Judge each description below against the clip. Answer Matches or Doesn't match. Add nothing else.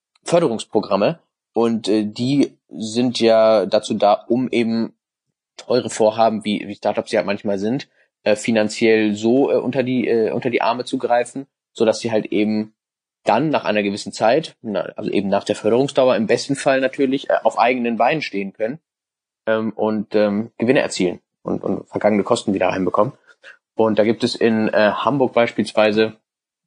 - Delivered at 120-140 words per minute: Doesn't match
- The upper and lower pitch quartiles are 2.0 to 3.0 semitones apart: Matches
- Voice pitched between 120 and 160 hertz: Doesn't match